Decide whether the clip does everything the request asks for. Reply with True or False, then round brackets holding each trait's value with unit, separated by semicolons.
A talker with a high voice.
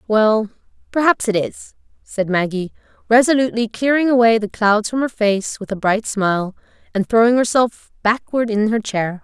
True (220 Hz)